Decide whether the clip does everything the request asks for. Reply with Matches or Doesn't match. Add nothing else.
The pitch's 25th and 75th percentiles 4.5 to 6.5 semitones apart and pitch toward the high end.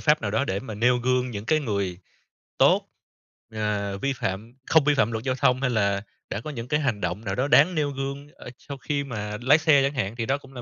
Doesn't match